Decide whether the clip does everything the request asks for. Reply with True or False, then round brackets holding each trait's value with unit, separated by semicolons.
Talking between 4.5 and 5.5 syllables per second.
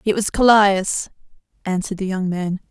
True (5.0 syllables/s)